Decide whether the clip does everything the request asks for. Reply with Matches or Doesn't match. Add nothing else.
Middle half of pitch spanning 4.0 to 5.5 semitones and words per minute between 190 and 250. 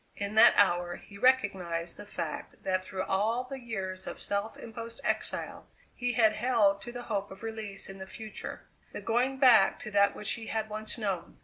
Doesn't match